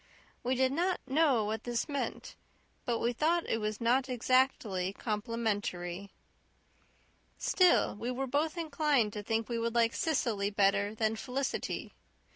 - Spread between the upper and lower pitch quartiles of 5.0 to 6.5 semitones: No, average, 4.2 semitones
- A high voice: Yes, high, 235 Hz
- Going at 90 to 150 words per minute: Yes, average, 140 wpm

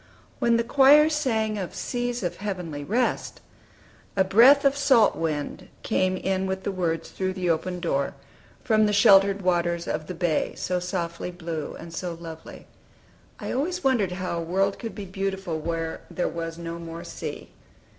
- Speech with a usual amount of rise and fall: Yes, average, 4.3 semitones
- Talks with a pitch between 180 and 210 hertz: Yes, medium, 185 Hz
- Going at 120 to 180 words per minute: Yes, average, 170 wpm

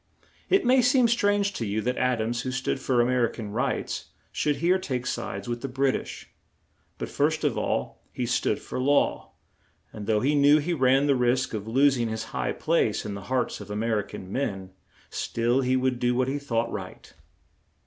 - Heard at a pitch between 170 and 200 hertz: No, low, 125 Hz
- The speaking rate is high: Yes, fast, 215 wpm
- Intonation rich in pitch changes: No, average, 3.9 semitones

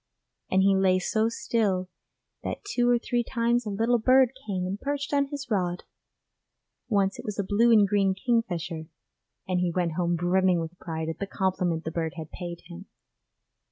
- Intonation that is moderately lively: Yes, average, 4.7 semitones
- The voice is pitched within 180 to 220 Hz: Yes, high, 190 Hz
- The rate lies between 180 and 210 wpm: Yes, average, 185 wpm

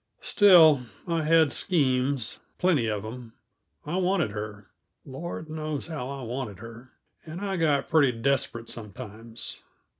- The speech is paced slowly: Yes, slow, 130 wpm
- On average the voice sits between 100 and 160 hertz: Yes, low, 135 Hz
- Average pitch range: No, wide, 5.8 semitones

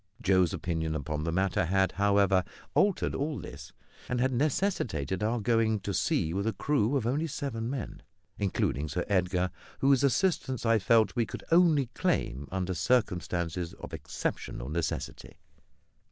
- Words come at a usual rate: Yes, average, 150 wpm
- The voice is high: No, low, 100 Hz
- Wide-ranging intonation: Yes, wide, 6.4 semitones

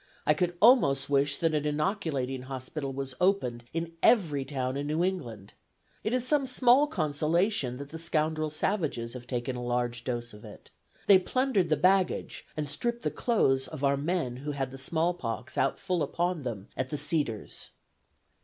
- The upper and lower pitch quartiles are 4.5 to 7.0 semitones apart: Yes, wide, 5.4 semitones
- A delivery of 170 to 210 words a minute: Yes, average, 180 wpm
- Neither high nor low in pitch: Yes, medium, 150 Hz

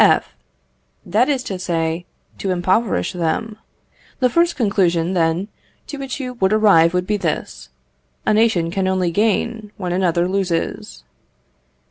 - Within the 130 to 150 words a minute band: Yes, average, 140 wpm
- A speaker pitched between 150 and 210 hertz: Yes, high, 190 Hz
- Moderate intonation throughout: Yes, average, 4.2 semitones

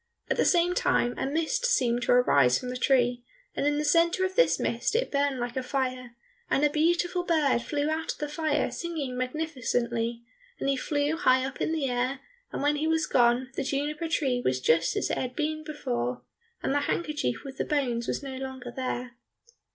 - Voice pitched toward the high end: Yes, very high, 275 Hz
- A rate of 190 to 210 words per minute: Yes, fast, 205 wpm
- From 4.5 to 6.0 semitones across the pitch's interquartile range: No, average, 3.8 semitones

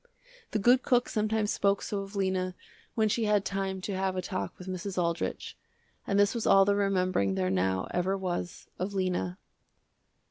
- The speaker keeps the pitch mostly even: Yes, narrow, 1.9 semitones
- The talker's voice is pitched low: No, high, 190 Hz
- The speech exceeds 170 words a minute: Yes, average, 180 wpm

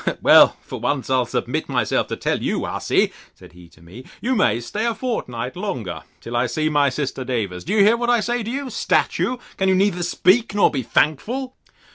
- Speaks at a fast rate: Yes, fast, 210 wpm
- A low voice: No, medium, 170 Hz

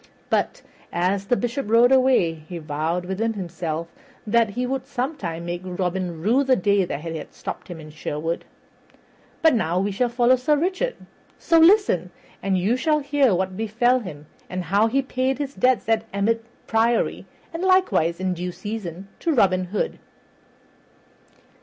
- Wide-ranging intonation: Yes, wide, 6.3 semitones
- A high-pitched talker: Yes, high, 205 Hz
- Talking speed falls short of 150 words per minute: No, average, 160 wpm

